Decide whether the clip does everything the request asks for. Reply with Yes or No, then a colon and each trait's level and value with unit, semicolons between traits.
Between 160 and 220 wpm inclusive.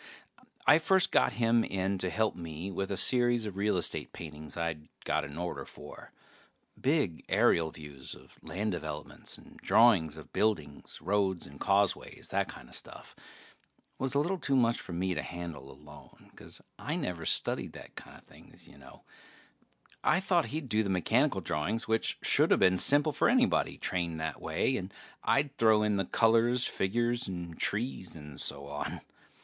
Yes: average, 170 wpm